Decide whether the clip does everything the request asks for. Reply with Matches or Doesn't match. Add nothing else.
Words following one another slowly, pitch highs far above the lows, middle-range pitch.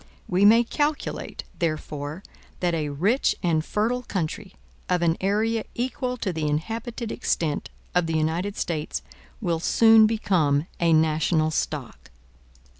Matches